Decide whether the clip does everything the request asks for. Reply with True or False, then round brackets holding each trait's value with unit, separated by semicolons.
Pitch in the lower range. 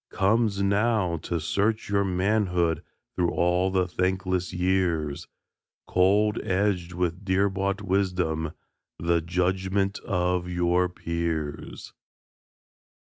True (90 Hz)